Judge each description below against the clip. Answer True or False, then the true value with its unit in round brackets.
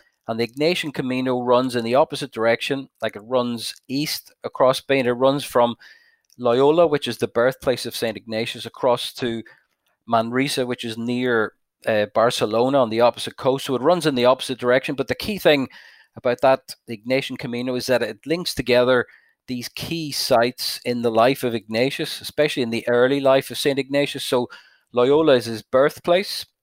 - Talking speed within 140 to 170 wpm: False (180 wpm)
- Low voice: True (125 Hz)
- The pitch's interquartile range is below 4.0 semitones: True (2.5 semitones)